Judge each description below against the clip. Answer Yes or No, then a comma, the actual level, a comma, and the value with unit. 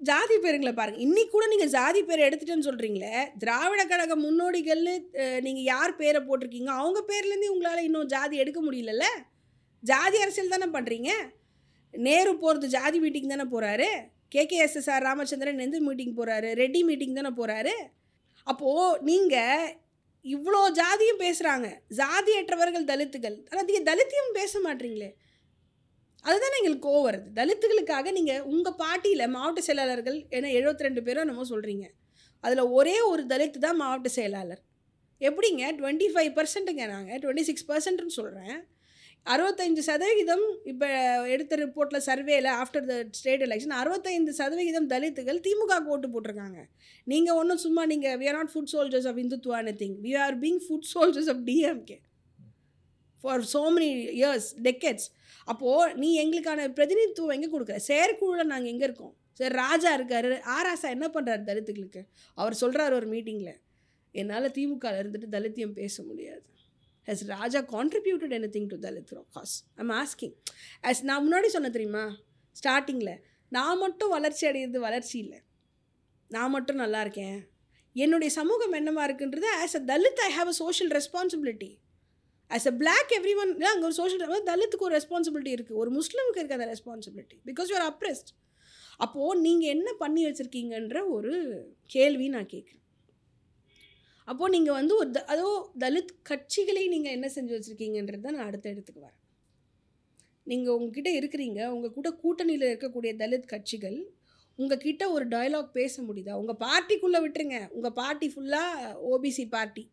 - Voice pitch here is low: No, very high, 280 Hz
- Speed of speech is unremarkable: No, fast, 145 wpm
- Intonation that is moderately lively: No, wide, 5.7 semitones